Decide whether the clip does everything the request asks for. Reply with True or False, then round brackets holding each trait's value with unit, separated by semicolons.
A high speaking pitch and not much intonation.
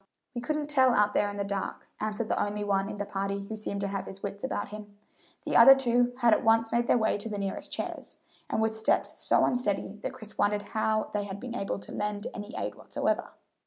True (210 Hz; 2.2 semitones)